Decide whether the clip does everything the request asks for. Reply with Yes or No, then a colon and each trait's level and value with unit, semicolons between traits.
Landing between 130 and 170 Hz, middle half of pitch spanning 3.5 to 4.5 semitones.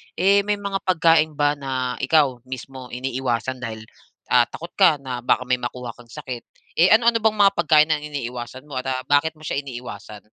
Yes: low, 135 Hz; average, 4.1 semitones